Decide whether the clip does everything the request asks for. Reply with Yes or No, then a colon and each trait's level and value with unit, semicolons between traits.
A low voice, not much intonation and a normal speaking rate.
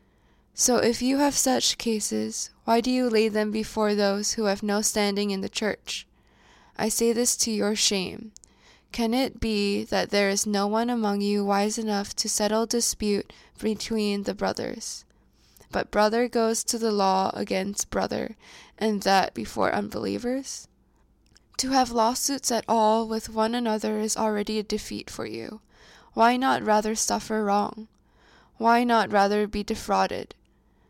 No: high, 215 Hz; narrow, 2.0 semitones; average, 155 wpm